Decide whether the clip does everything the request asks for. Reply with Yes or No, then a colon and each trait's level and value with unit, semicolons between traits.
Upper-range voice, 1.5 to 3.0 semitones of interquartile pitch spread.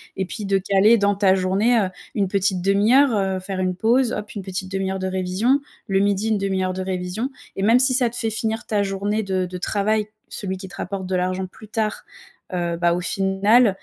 Yes: high, 195 Hz; narrow, 2.4 semitones